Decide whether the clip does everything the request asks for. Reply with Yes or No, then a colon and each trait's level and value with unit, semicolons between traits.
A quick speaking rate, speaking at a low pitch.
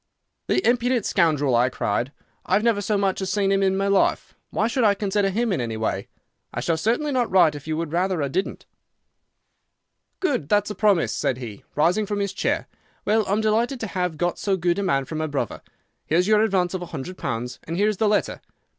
No: fast, 220 wpm; high, 190 Hz